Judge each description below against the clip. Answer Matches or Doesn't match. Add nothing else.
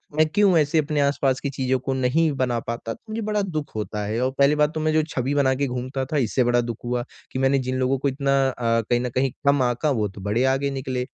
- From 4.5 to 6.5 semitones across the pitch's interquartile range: Doesn't match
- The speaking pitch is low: Matches